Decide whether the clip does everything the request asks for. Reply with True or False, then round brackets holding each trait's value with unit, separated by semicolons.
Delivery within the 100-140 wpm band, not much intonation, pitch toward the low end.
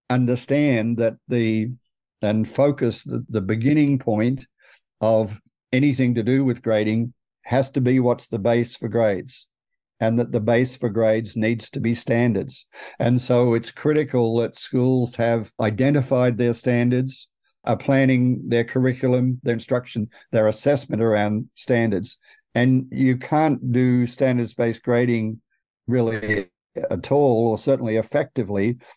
True (135 wpm; 2.1 semitones; 120 Hz)